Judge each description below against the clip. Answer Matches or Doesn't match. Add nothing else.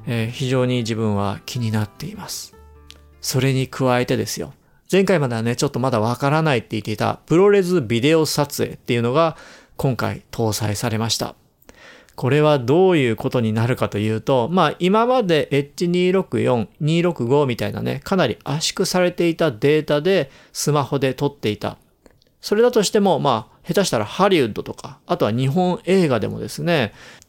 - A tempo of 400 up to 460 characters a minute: Doesn't match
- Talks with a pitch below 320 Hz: Matches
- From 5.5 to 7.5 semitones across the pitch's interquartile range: Matches